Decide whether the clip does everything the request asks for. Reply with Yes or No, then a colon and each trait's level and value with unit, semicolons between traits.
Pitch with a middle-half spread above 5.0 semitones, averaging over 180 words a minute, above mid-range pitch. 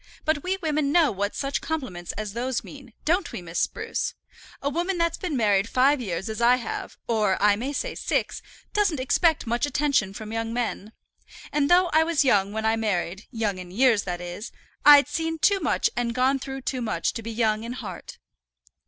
Yes: wide, 5.6 semitones; average, 200 wpm; high, 245 Hz